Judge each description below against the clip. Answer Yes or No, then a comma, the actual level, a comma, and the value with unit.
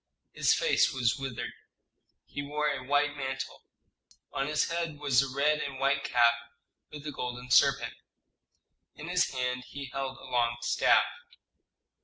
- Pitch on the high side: No, low, 135 Hz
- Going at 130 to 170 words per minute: Yes, average, 150 wpm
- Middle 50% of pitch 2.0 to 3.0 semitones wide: Yes, narrow, 2.4 semitones